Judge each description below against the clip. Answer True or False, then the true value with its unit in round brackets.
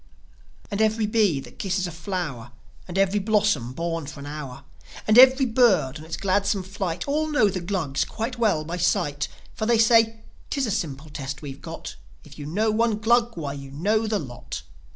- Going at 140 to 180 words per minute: False (195 wpm)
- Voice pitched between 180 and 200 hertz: True (190 Hz)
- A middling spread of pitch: False (6.5 semitones)